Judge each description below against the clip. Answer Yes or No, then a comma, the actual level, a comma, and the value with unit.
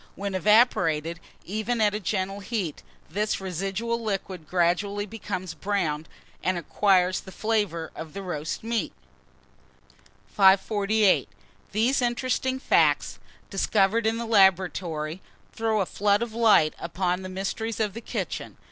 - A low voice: No, high, 195 Hz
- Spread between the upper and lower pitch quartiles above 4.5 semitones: No, average, 3.3 semitones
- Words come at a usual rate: No, slow, 125 wpm